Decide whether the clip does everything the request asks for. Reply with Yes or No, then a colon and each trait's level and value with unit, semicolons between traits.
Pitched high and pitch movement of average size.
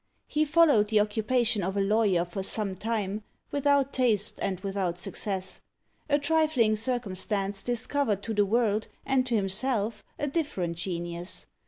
Yes: high, 215 Hz; average, 4.7 semitones